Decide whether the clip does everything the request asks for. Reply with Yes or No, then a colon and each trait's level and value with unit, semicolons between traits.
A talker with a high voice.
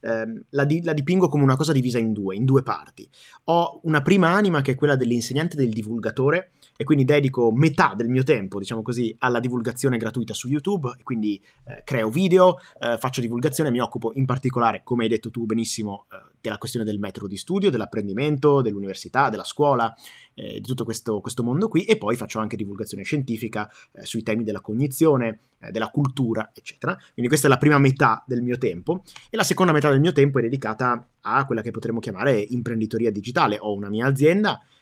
No: low, 125 Hz